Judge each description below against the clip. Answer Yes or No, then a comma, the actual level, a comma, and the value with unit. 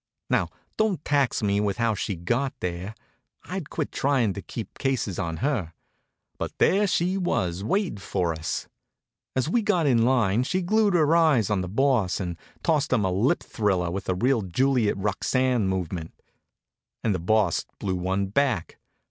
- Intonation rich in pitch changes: Yes, wide, 6.9 semitones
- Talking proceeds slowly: No, average, 170 wpm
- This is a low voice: Yes, low, 110 Hz